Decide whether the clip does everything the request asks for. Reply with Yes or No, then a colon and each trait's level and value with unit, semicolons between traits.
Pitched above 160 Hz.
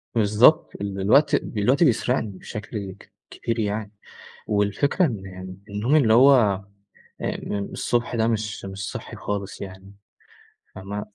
No: low, 105 Hz